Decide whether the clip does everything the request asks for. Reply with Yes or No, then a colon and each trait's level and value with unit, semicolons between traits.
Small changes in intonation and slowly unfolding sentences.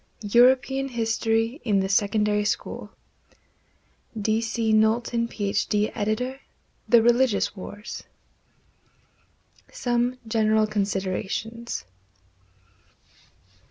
Yes: narrow, 2.3 semitones; slow, 75 wpm